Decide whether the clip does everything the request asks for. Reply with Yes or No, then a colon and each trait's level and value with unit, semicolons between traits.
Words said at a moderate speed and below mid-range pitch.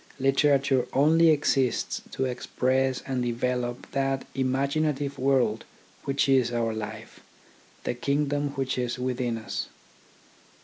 No: slow, 115 wpm; low, 130 Hz